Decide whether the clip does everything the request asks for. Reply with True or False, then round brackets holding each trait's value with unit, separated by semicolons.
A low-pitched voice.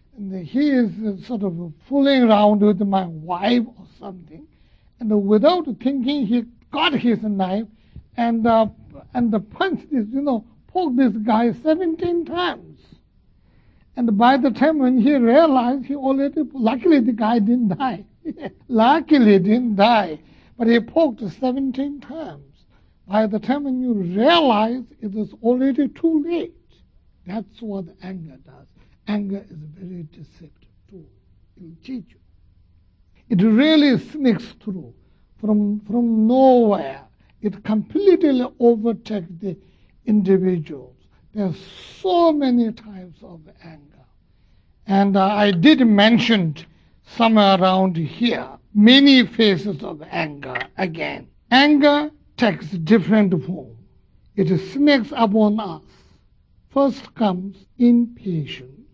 False (220 Hz)